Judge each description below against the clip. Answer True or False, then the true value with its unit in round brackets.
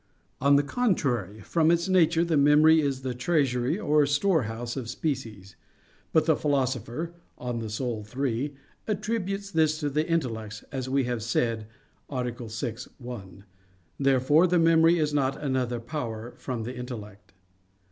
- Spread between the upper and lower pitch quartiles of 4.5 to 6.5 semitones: True (4.9 semitones)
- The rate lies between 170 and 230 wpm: False (145 wpm)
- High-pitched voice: False (135 Hz)